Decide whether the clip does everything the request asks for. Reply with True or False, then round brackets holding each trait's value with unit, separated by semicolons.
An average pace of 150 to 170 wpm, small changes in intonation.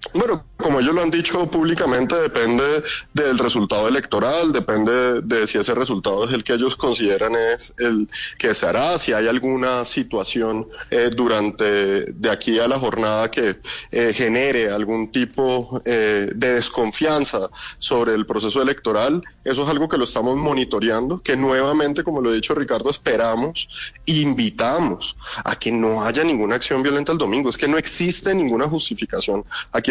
False (165 wpm; 5.3 semitones)